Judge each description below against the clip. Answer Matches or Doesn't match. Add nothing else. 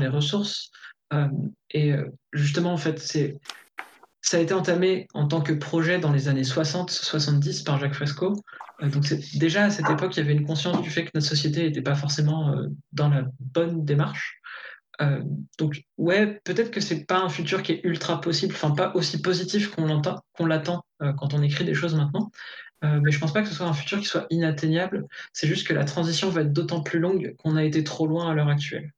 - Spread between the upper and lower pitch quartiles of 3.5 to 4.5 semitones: Doesn't match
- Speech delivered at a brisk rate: Matches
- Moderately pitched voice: Matches